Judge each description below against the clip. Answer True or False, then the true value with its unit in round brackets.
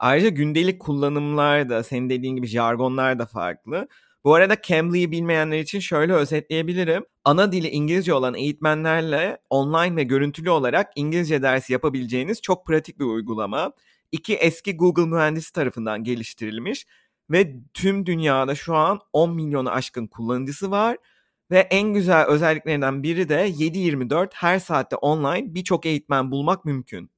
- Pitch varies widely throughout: False (4.7 semitones)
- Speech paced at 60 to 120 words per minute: False (135 wpm)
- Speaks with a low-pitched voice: False (155 Hz)